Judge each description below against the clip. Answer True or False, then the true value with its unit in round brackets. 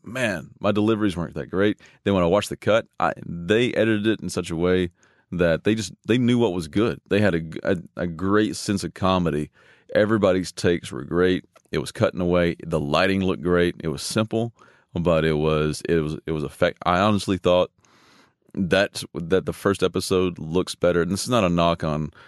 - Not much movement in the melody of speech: False (3.2 semitones)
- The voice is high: False (90 Hz)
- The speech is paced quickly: True (210 wpm)